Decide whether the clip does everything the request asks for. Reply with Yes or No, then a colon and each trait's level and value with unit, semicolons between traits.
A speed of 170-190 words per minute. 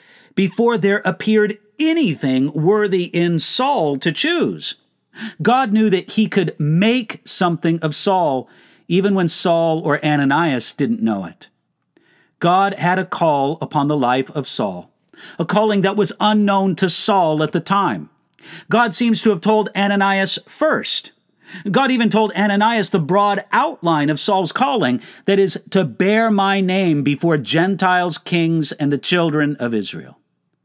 No: average, 150 wpm